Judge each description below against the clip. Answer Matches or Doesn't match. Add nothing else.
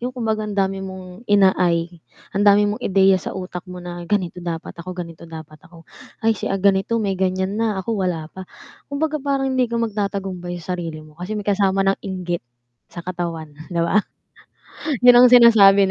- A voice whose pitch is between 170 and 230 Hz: Matches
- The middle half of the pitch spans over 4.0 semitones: Doesn't match